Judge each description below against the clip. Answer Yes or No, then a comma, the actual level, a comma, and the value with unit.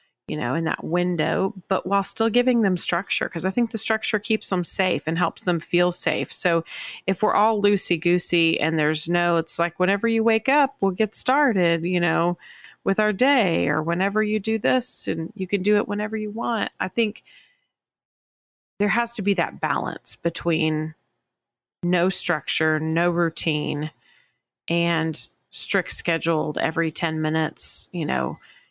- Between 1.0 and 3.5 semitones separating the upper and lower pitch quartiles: No, average, 4.2 semitones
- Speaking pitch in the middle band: Yes, medium, 180 Hz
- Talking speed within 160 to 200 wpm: Yes, average, 170 wpm